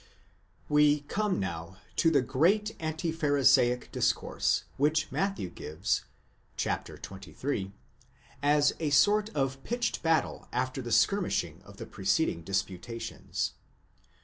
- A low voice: No, medium, 145 Hz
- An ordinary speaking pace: No, slow, 120 wpm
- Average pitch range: No, wide, 6.6 semitones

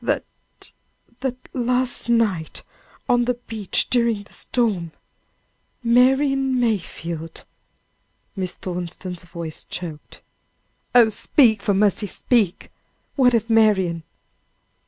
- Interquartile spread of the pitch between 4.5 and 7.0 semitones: Yes, average, 5.3 semitones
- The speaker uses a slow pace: Yes, slow, 100 wpm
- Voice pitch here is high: Yes, high, 220 Hz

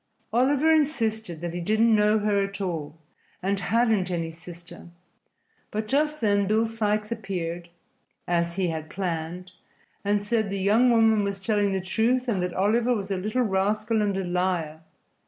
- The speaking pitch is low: No, high, 200 Hz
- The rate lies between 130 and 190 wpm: Yes, average, 165 wpm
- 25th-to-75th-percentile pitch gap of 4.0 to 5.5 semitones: No, average, 3.6 semitones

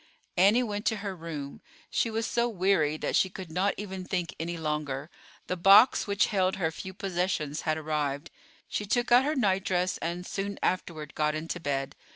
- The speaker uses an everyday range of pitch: Yes, average, 4.3 semitones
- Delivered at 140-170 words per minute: No, average, 185 wpm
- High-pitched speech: No, medium, 180 Hz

